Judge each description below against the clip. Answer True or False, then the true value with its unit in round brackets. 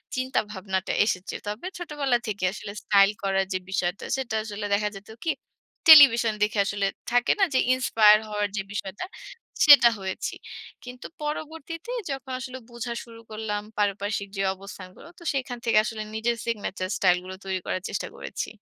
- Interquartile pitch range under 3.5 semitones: False (4.4 semitones)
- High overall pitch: True (215 Hz)